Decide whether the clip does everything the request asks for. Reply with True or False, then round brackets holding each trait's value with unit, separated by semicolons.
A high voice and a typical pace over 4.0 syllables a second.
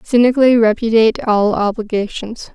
True (225 Hz; 5.4 syllables/s)